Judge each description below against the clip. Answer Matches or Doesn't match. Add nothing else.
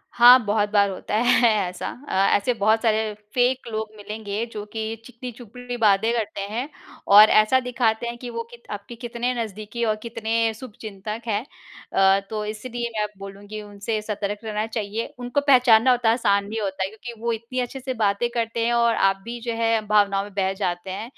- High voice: Matches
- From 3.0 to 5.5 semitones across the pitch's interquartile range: Doesn't match